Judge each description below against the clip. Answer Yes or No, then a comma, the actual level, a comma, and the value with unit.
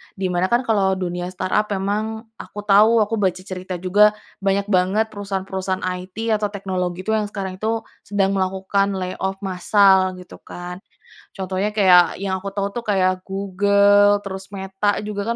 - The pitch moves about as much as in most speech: No, narrow, 1.7 semitones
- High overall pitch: Yes, high, 195 Hz